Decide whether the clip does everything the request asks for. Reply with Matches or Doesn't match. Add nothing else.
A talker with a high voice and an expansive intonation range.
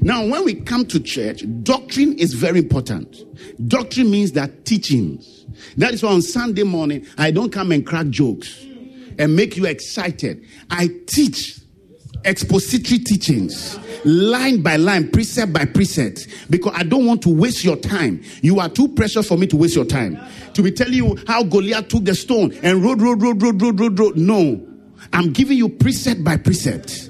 Matches